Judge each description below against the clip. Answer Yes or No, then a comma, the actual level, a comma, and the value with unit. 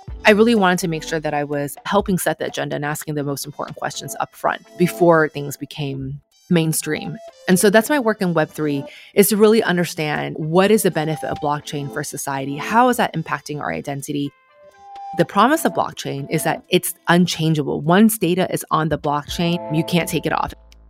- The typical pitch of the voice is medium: Yes, medium, 160 Hz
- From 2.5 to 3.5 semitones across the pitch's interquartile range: No, average, 4.3 semitones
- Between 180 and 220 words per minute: Yes, average, 200 wpm